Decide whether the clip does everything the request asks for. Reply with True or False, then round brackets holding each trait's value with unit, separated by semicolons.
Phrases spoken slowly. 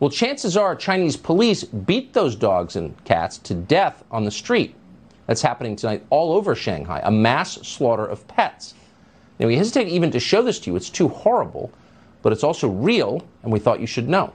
False (200 wpm)